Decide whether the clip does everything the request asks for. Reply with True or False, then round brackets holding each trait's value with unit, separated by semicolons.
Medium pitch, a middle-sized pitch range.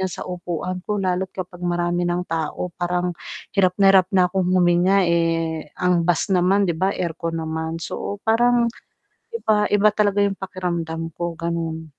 False (180 Hz; 2.2 semitones)